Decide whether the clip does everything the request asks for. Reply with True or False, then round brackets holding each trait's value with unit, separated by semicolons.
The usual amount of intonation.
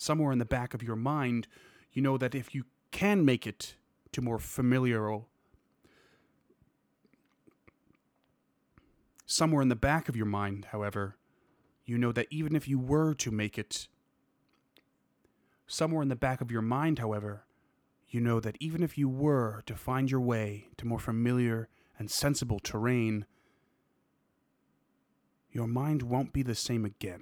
True (3.7 semitones)